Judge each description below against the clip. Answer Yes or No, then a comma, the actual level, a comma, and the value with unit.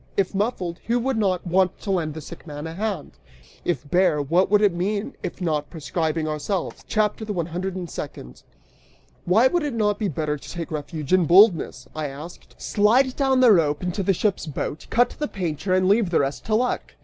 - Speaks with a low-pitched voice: No, medium, 185 Hz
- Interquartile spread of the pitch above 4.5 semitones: Yes, average, 4.9 semitones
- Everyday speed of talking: No, fast, 210 wpm